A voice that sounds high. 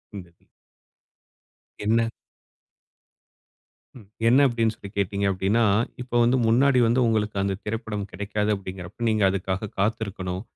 No: low, 105 Hz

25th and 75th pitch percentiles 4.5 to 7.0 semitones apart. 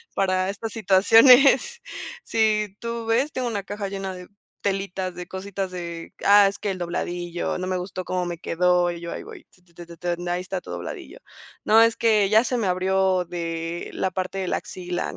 No: average, 2.9 semitones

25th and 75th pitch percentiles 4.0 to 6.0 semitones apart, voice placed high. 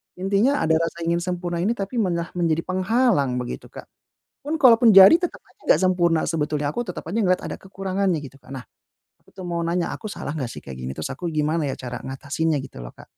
No: average, 4.5 semitones; medium, 170 Hz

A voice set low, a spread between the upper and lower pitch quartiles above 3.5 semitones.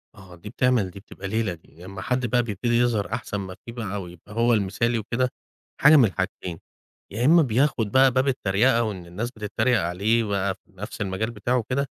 Yes: low, 110 Hz; average, 3.9 semitones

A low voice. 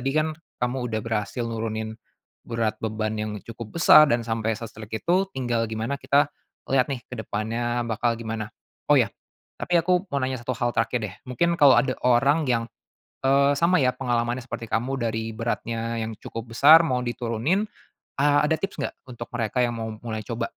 Yes: low, 120 Hz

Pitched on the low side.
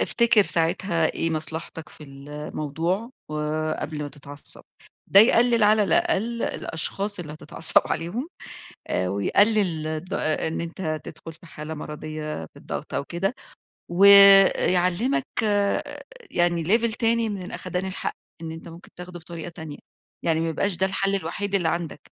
No: medium, 170 Hz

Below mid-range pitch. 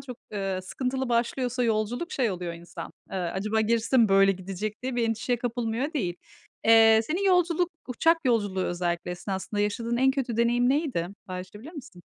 No: high, 225 Hz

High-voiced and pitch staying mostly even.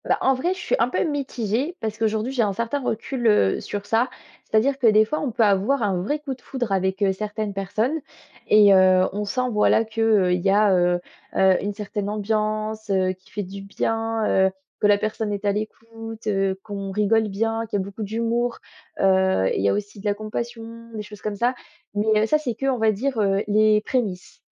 Yes: high, 215 Hz; narrow, 2.3 semitones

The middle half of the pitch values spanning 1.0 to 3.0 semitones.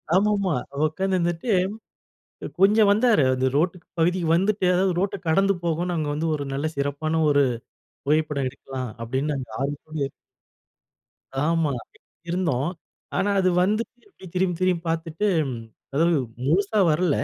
No: average, 4.4 semitones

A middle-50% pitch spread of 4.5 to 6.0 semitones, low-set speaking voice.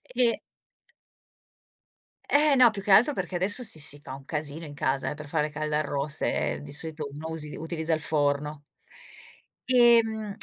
No: average, 5.2 semitones; medium, 155 Hz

